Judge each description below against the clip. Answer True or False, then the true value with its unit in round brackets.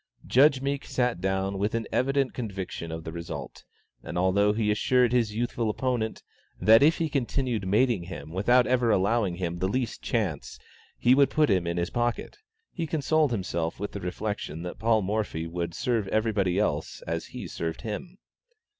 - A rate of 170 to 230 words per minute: True (175 wpm)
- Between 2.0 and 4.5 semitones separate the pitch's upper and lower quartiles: False (5.4 semitones)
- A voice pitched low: True (105 Hz)